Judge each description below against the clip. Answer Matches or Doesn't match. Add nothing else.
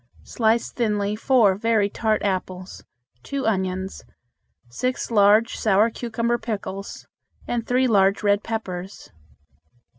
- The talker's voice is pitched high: Matches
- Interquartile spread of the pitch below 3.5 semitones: Matches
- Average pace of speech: Doesn't match